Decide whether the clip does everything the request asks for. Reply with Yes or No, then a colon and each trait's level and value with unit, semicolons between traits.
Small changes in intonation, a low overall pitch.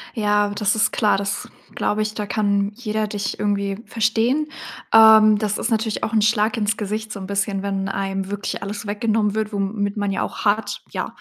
No: narrow, 1.4 semitones; high, 210 Hz